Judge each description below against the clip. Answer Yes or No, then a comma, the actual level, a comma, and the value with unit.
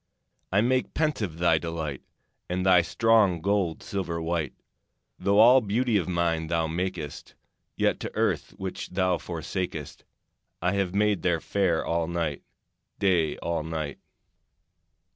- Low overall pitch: Yes, very low, 90 Hz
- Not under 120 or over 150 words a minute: Yes, slow, 135 wpm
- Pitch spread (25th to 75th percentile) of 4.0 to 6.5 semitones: No, average, 3.4 semitones